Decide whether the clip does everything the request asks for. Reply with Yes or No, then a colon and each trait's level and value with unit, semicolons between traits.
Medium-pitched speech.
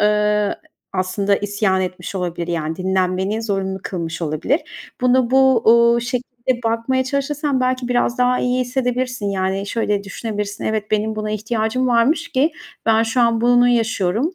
No: high, 225 Hz